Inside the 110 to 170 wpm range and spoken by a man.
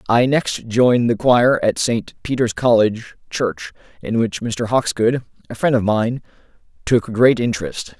Yes: average, 160 wpm; male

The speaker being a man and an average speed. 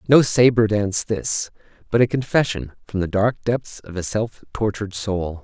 Yes: male; average, 175 wpm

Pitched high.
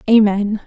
Yes: high, 210 Hz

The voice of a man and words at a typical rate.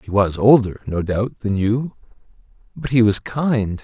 Yes: male; average, 170 wpm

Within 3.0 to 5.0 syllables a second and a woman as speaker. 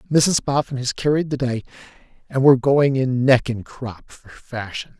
No: 4.6 syllables/s; male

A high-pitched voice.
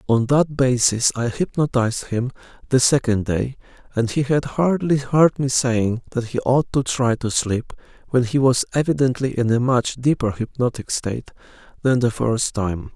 No: low, 125 Hz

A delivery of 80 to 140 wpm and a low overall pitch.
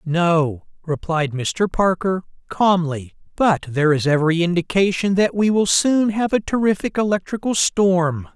No: slow, 135 wpm; medium, 180 Hz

